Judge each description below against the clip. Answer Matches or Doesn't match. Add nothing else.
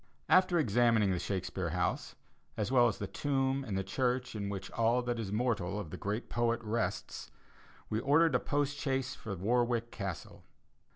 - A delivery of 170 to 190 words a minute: Matches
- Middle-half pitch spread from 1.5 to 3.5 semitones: Doesn't match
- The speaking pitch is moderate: Doesn't match